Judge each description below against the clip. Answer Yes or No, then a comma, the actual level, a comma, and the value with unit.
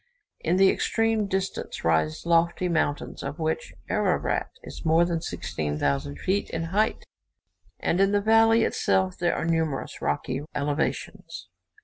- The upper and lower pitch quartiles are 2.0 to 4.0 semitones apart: No, average, 5.0 semitones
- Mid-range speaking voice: Yes, medium, 170 Hz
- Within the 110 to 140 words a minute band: Yes, slow, 135 wpm